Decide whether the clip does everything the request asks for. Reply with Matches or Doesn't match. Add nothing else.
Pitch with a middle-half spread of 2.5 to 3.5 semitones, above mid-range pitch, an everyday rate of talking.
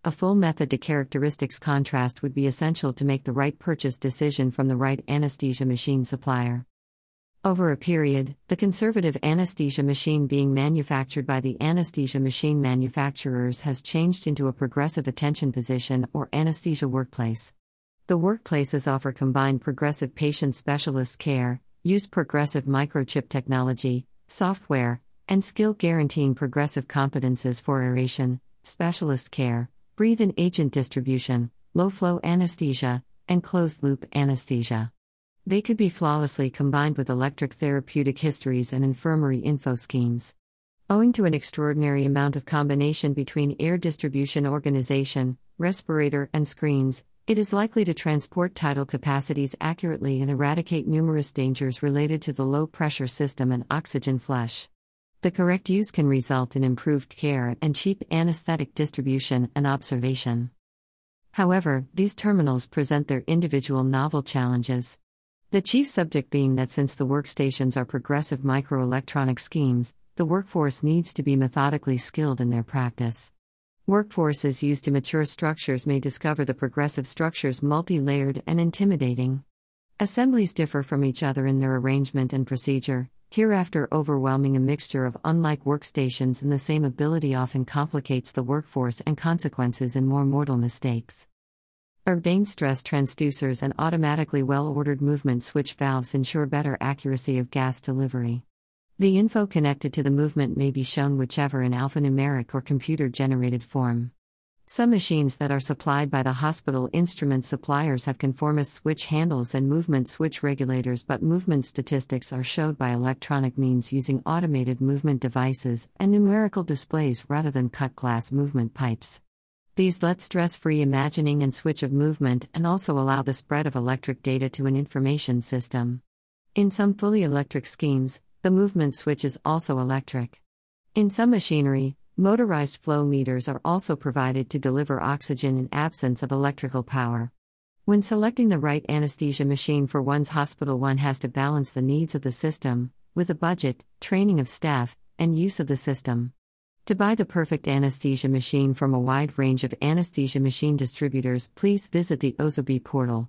Doesn't match